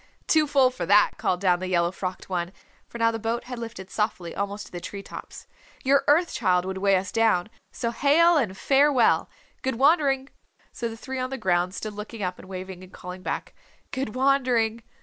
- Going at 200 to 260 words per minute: Yes, fast, 205 wpm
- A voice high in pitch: Yes, high, 225 Hz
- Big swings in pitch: Yes, wide, 5.9 semitones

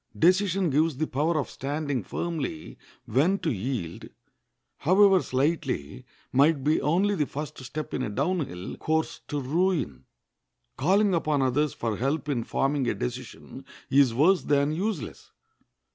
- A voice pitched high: No, medium, 150 Hz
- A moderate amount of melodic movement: Yes, average, 4.2 semitones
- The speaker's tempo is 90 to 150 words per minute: Yes, average, 145 wpm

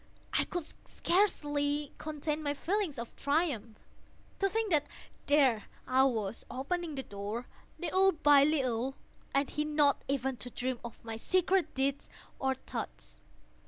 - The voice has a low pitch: No, very high, 285 Hz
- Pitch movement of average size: Yes, average, 3.8 semitones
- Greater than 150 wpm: No, average, 140 wpm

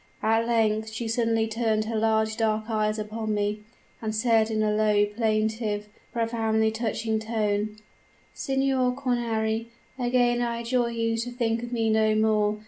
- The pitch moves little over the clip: Yes, narrow, 1.4 semitones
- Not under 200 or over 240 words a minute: No, average, 150 wpm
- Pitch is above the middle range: Yes, high, 220 Hz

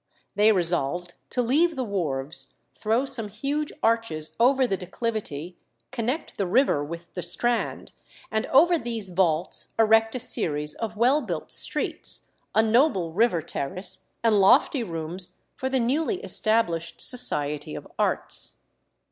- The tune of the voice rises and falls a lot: Yes, wide, 6.2 semitones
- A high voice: Yes, high, 220 Hz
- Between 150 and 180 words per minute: No, average, 140 wpm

